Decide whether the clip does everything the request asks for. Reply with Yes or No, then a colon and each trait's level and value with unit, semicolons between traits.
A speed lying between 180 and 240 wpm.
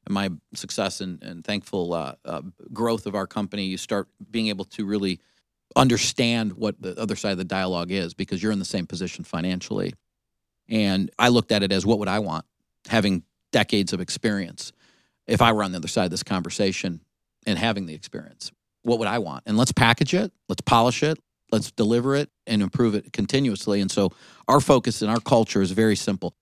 Yes: average, 200 wpm